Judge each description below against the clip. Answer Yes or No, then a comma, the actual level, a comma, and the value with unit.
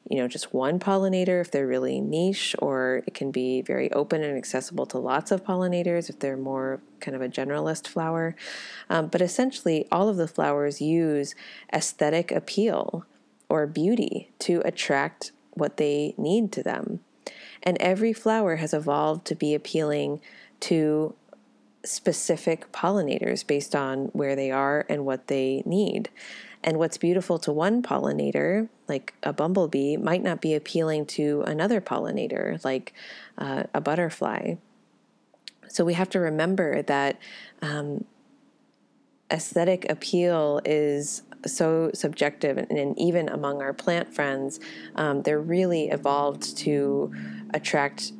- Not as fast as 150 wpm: Yes, average, 140 wpm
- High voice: No, medium, 155 Hz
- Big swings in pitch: No, average, 4.1 semitones